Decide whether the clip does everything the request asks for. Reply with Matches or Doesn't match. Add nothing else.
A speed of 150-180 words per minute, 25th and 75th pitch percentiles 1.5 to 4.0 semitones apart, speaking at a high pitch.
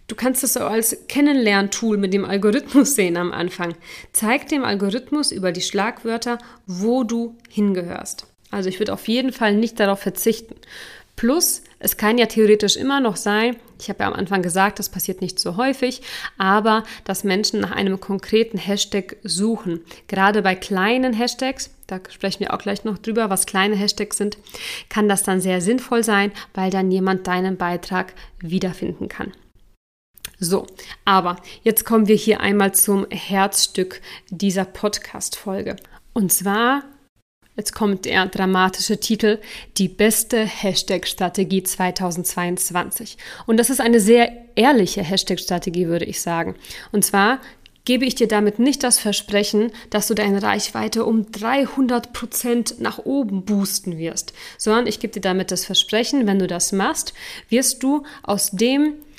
Matches